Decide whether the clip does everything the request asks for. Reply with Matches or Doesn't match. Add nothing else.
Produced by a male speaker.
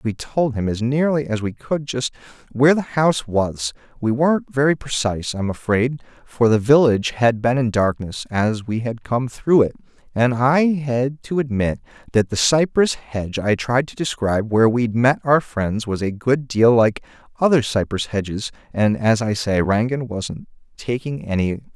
Matches